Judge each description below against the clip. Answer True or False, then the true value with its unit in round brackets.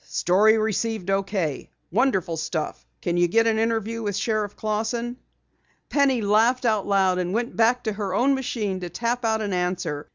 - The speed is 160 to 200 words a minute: True (165 wpm)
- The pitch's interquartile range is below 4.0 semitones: True (3.6 semitones)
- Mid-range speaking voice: False (215 Hz)